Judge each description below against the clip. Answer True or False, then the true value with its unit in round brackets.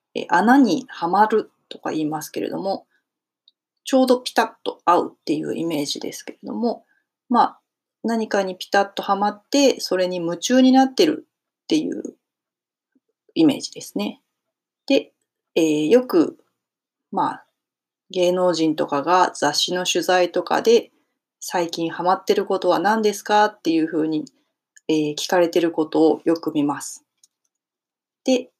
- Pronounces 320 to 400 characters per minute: False (275 characters per minute)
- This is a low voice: False (200 Hz)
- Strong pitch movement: True (7.3 semitones)